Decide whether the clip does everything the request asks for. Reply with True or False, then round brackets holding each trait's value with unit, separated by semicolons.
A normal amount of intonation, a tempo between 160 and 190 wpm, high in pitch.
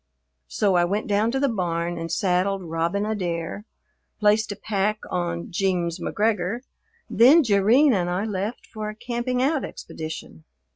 False (4.0 semitones; 150 wpm; 200 Hz)